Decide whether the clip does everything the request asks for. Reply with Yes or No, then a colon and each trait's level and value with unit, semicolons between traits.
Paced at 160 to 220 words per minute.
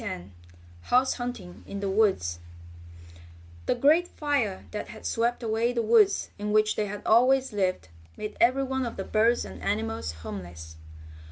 Yes: average, 165 wpm